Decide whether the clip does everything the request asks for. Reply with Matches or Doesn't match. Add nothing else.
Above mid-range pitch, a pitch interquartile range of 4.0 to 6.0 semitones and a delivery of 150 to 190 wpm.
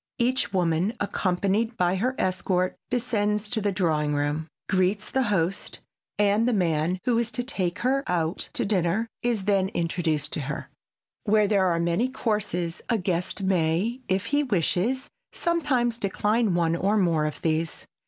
Matches